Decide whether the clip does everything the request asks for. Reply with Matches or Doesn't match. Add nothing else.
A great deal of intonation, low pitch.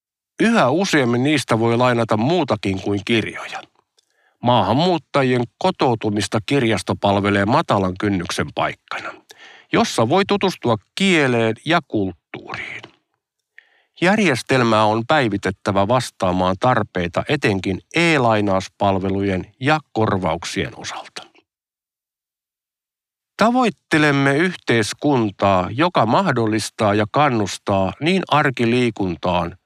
Matches